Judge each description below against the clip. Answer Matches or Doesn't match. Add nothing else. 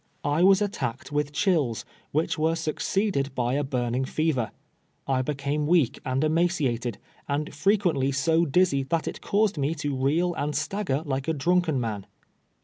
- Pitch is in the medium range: Matches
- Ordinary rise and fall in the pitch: Matches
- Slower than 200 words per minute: Matches